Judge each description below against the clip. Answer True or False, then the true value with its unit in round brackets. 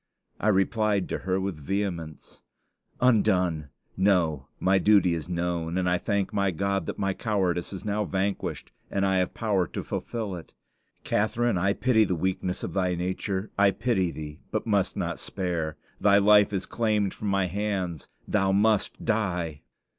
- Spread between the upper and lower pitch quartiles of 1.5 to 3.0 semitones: True (2.5 semitones)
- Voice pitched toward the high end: False (95 Hz)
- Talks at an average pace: True (165 wpm)